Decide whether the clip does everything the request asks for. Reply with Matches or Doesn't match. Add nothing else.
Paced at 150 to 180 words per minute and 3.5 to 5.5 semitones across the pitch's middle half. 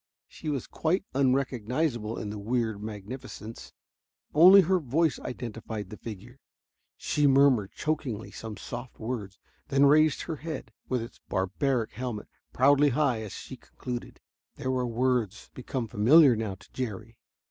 Doesn't match